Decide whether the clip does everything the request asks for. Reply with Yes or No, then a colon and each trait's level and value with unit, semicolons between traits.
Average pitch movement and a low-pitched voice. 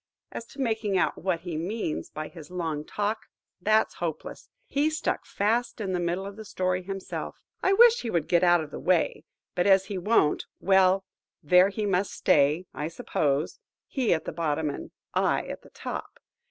No: average, 4.1 semitones; medium, 185 Hz